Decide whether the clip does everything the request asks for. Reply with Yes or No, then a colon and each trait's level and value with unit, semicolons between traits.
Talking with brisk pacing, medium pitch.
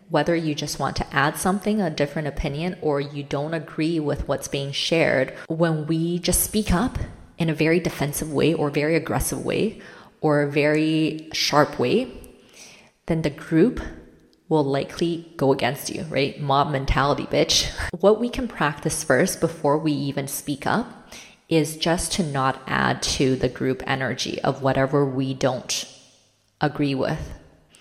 No: average, 160 wpm; medium, 150 Hz